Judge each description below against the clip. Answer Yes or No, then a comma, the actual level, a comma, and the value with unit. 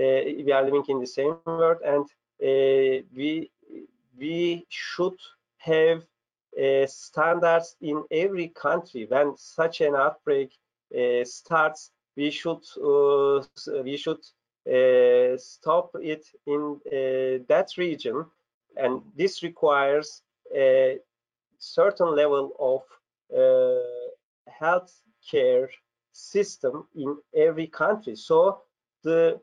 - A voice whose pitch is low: No, medium, 165 Hz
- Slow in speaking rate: Yes, slow, 105 wpm